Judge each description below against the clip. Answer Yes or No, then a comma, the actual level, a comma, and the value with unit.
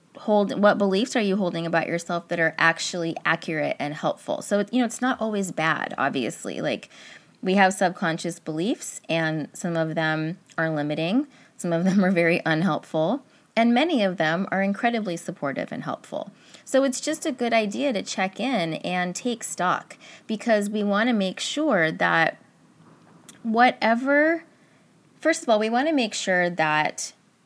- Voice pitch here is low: No, high, 195 Hz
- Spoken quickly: No, average, 170 wpm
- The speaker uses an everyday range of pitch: No, wide, 6.2 semitones